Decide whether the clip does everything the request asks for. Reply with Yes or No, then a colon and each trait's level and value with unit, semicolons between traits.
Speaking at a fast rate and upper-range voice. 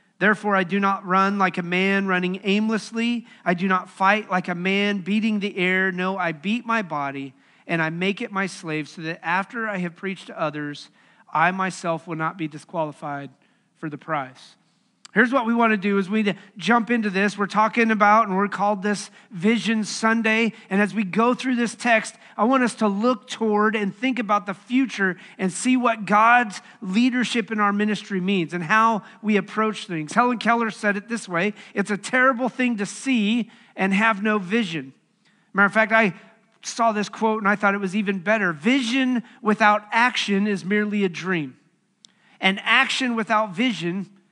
No: average, 195 wpm; high, 205 Hz